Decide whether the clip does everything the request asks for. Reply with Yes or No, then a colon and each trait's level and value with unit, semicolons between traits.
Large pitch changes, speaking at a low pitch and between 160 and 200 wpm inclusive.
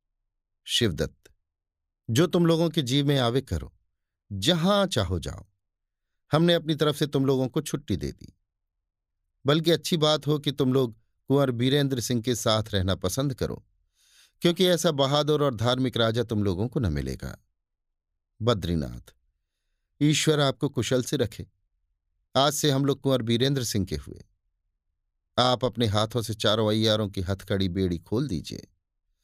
No: wide, 7.2 semitones; low, 110 Hz; average, 150 wpm